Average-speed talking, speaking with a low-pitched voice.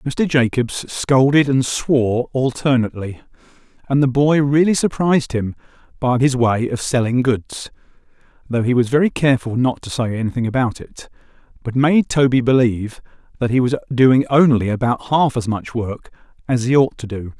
Yes: average, 165 wpm; low, 125 Hz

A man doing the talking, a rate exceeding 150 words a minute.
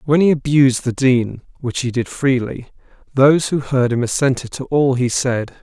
Yes: male; average, 190 wpm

